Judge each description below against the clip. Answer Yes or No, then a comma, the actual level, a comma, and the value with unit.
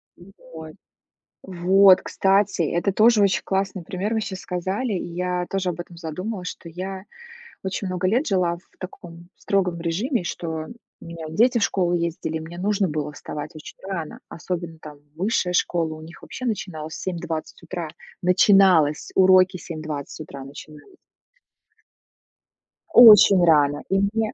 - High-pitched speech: No, medium, 180 Hz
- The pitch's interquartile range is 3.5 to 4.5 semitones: No, average, 2.9 semitones